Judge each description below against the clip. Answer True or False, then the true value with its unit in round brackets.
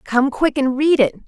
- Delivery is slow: False (235 wpm)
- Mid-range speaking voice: False (275 Hz)